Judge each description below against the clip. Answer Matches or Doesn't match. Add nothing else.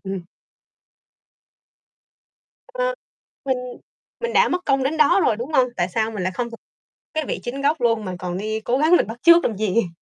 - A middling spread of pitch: Doesn't match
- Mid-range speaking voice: Doesn't match